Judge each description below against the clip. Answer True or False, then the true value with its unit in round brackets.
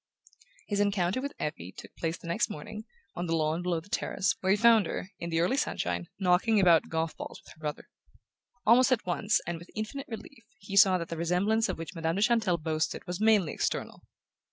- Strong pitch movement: False (4.6 semitones)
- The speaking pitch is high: False (180 Hz)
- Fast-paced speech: True (210 wpm)